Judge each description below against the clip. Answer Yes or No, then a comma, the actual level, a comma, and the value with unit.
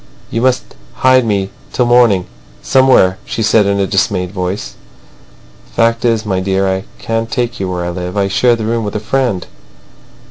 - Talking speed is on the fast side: No, average, 185 wpm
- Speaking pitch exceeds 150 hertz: No, low, 105 Hz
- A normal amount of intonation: Yes, average, 3.6 semitones